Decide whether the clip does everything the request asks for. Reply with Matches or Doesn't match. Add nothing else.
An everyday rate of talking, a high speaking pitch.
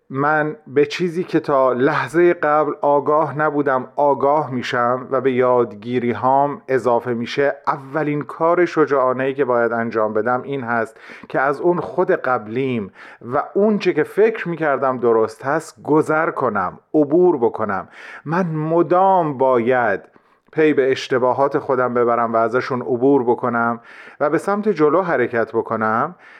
Doesn't match